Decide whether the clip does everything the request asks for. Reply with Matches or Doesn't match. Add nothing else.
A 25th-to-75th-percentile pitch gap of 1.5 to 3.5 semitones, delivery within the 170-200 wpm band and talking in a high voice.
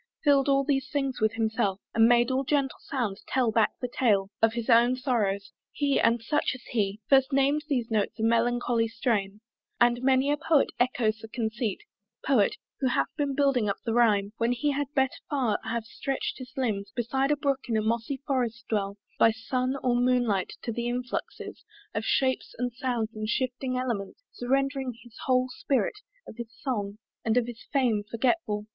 Matches